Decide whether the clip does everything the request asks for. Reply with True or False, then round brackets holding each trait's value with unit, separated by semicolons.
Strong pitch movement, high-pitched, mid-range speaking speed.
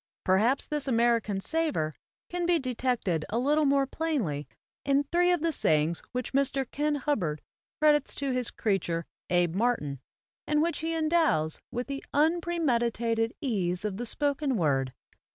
True (7.5 semitones; 255 Hz; 150 wpm)